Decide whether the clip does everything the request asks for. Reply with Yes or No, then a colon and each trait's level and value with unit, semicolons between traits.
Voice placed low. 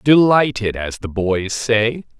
Yes: low, 115 Hz